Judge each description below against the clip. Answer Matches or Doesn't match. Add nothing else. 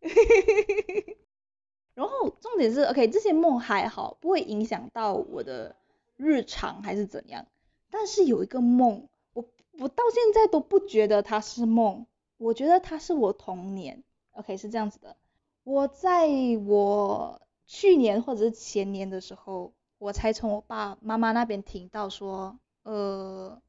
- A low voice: Doesn't match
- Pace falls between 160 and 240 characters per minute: Matches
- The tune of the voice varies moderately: Doesn't match